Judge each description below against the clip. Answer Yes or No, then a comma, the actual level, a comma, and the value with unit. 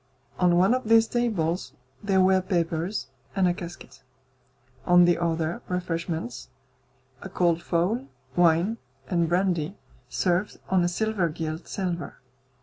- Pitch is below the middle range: No, medium, 175 Hz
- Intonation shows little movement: Yes, narrow, 2.3 semitones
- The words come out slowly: Yes, slow, 130 wpm